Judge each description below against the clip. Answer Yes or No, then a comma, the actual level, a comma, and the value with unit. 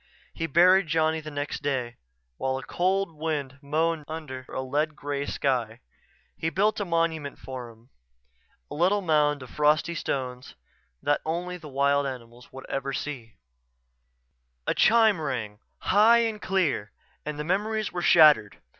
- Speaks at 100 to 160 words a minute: Yes, average, 150 wpm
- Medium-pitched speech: Yes, medium, 150 Hz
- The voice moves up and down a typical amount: Yes, average, 4.3 semitones